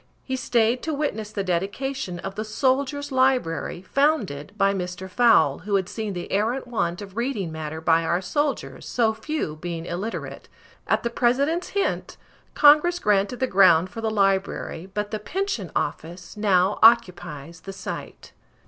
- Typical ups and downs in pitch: No, wide, 6.2 semitones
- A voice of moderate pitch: No, high, 210 Hz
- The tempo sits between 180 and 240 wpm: No, average, 155 wpm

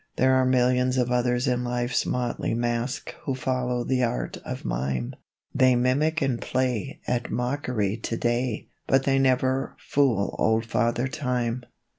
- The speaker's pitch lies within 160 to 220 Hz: No, low, 125 Hz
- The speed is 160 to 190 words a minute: No, average, 145 wpm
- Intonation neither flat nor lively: No, narrow, 1.5 semitones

